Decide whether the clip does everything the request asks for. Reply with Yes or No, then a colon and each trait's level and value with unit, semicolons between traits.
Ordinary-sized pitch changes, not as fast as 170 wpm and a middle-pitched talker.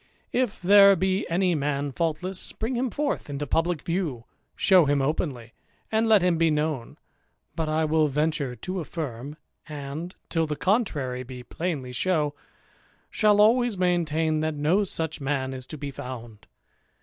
Yes: average, 4.8 semitones; average, 155 wpm; medium, 155 Hz